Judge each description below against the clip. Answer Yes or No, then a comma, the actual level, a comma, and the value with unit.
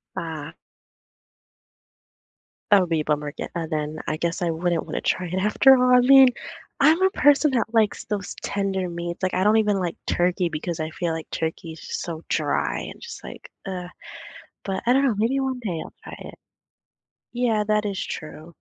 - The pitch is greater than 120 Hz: Yes, medium, 185 Hz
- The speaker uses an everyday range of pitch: No, wide, 5.7 semitones